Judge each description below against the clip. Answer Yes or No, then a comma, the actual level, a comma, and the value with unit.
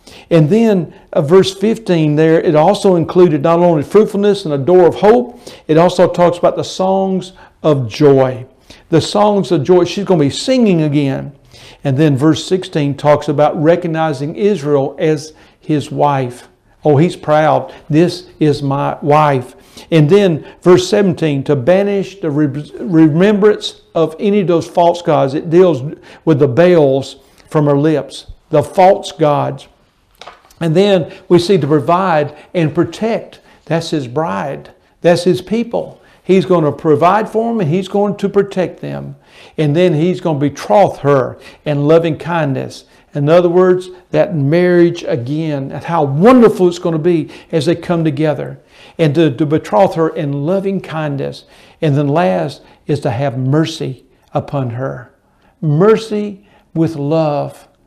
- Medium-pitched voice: Yes, medium, 165 Hz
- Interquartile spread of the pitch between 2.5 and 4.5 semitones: Yes, average, 3.7 semitones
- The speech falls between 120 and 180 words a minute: Yes, average, 155 wpm